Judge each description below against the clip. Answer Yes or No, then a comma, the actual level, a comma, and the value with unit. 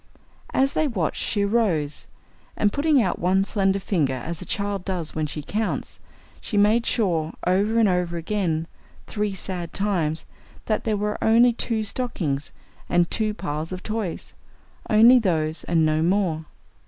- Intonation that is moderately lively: Yes, average, 4.6 semitones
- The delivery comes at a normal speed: Yes, average, 155 wpm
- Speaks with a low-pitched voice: No, high, 195 Hz